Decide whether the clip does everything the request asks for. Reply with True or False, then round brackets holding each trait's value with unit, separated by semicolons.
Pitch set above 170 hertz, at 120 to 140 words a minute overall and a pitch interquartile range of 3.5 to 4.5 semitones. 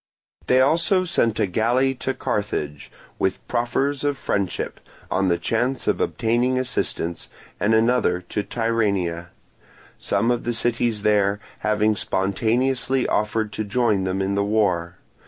False (110 Hz; 135 wpm; 3.9 semitones)